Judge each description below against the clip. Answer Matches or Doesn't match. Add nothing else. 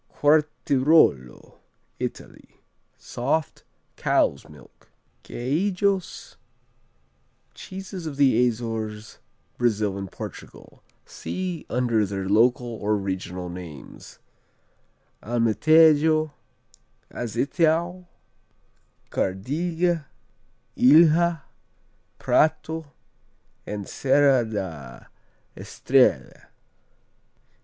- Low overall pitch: Matches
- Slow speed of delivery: Matches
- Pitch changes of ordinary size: Doesn't match